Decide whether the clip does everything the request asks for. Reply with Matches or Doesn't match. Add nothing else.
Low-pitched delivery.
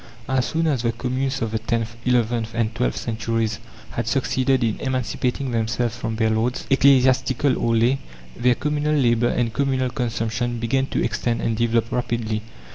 Matches